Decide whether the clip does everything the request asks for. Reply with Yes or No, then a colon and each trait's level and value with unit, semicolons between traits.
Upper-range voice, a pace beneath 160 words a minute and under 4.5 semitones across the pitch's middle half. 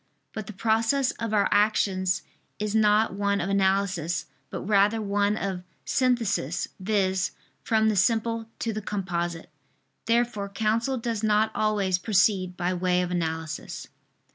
Yes: high, 205 Hz; average, 140 wpm; average, 2.8 semitones